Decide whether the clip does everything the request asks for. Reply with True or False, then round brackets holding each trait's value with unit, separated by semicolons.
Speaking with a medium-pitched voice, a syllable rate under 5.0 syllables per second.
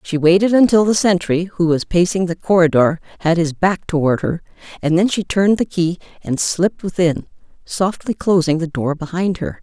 False (175 Hz; 5.2 syllables/s)